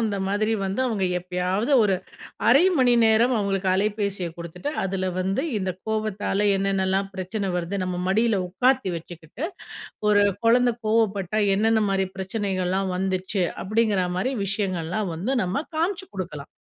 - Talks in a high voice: Yes, high, 195 Hz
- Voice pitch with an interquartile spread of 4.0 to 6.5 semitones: No, average, 2.8 semitones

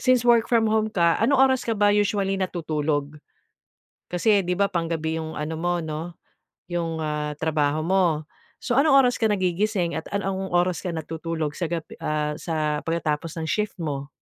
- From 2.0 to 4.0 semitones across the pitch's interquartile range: No, average, 4.5 semitones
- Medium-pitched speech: Yes, medium, 170 Hz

